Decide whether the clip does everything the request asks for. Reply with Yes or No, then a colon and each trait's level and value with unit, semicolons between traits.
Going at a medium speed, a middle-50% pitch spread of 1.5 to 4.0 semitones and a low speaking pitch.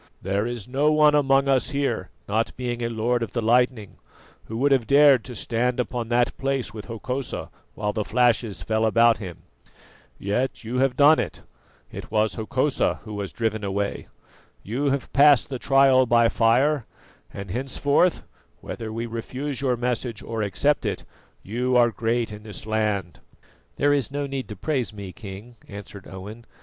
Yes: average, 170 wpm; average, 3.6 semitones; low, 120 Hz